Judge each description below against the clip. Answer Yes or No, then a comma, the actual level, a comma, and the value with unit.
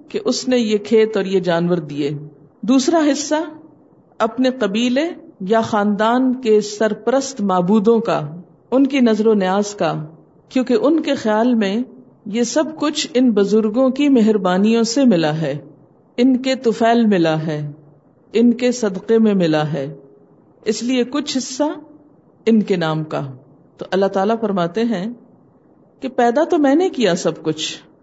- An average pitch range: No, wide, 6.4 semitones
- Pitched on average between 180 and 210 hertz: No, high, 220 Hz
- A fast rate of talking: No, average, 155 wpm